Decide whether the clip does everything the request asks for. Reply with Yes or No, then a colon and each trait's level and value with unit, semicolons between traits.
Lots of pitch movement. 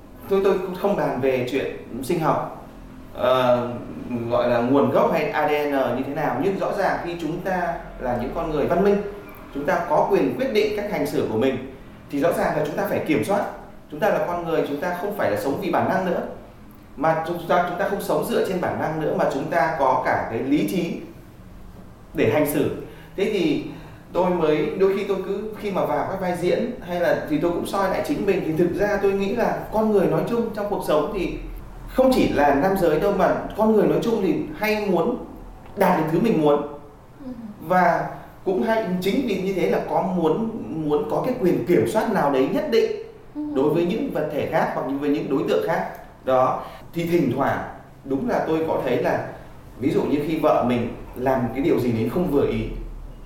Yes: wide, 5.8 semitones